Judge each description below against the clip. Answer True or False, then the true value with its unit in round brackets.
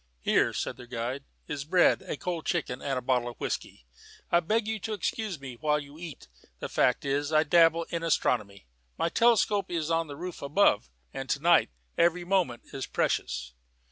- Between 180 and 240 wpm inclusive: True (190 wpm)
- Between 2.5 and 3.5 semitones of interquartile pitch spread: False (4.8 semitones)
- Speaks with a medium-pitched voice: True (155 Hz)